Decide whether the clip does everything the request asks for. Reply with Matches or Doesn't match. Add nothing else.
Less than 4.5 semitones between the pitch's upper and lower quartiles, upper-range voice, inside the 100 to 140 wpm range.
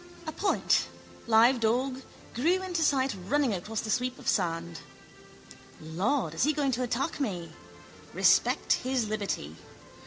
Doesn't match